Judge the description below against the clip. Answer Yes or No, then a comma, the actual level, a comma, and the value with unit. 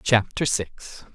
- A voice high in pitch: No, low, 115 Hz